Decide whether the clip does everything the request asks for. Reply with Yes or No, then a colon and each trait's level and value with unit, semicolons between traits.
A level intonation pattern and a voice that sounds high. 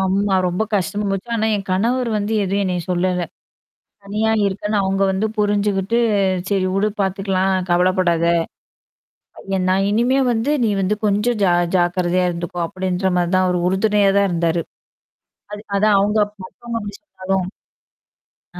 Yes: narrow, 2.1 semitones; high, 195 Hz